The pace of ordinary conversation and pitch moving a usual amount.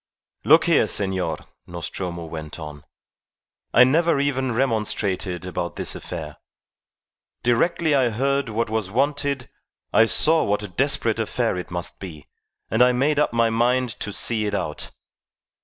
No: average, 145 wpm; wide, 6.4 semitones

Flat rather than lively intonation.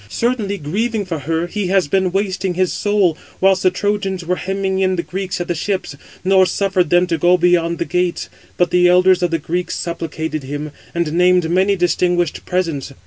Yes: narrow, 2.1 semitones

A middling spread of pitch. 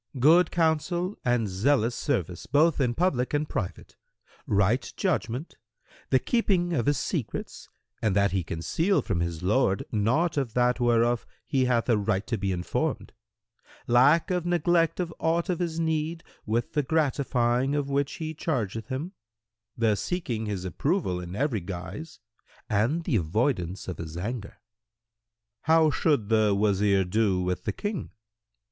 No: wide, 7.7 semitones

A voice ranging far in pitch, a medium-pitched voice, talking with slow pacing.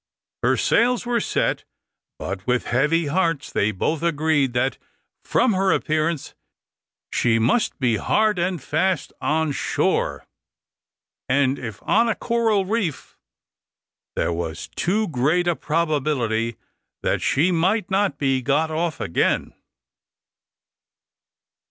Yes: wide, 6.3 semitones; medium, 155 Hz; slow, 120 wpm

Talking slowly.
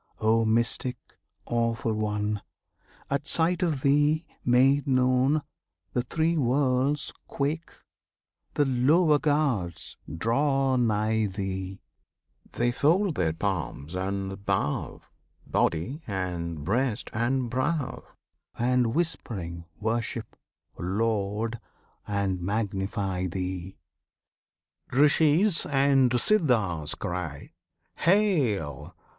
Yes: slow, 90 wpm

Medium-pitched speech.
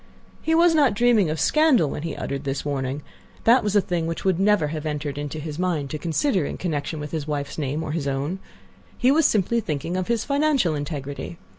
Yes: medium, 165 Hz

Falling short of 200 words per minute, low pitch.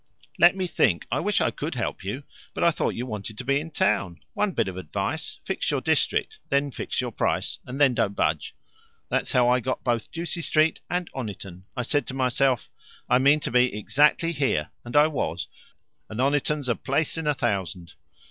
No: fast, 205 wpm; low, 130 Hz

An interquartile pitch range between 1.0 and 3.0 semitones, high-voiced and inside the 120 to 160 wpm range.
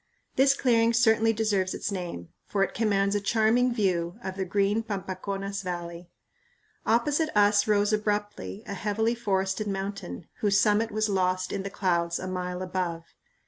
Yes: average, 2.7 semitones; high, 200 Hz; average, 155 wpm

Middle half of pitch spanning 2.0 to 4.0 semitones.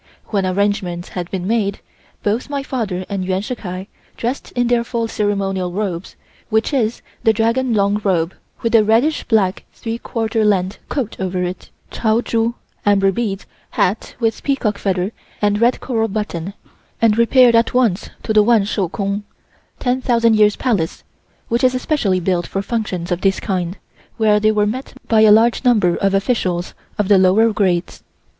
Yes: average, 3.3 semitones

